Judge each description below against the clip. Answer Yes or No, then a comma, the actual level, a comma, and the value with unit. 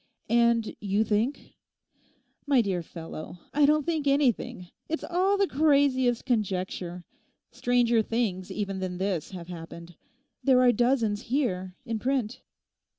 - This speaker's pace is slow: Yes, slow, 125 wpm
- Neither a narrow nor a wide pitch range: No, wide, 6.3 semitones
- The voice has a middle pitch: No, high, 230 Hz